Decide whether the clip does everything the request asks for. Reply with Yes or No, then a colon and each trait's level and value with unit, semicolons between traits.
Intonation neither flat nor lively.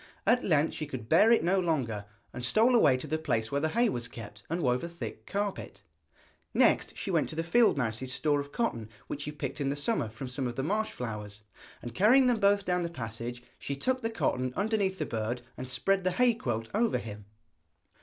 No: wide, 8.4 semitones